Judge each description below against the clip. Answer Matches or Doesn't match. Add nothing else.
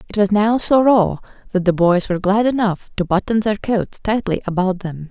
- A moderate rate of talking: Doesn't match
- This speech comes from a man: Doesn't match